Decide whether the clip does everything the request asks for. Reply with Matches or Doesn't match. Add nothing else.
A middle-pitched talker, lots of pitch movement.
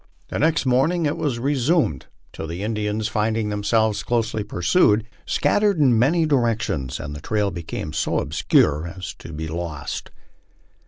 Doesn't match